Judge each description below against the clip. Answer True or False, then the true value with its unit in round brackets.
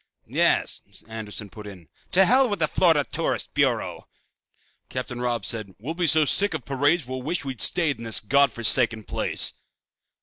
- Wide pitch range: True (6.1 semitones)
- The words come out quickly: False (170 wpm)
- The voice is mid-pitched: False (130 Hz)